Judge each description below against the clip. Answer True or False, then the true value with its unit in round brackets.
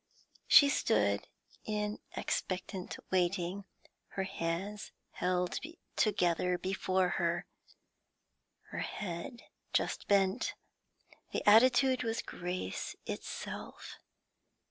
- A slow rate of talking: True (80 wpm)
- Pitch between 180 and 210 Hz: True (190 Hz)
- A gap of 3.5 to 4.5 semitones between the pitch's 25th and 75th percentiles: False (2.8 semitones)